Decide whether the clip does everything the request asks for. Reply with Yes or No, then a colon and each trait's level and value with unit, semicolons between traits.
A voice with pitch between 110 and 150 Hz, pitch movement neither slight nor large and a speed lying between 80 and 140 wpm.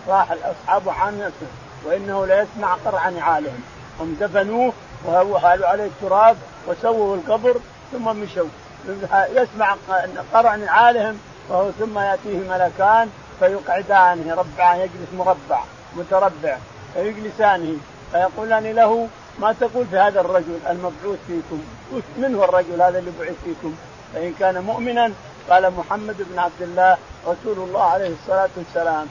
No: medium, 185 Hz; average, 3.4 semitones; average, 120 wpm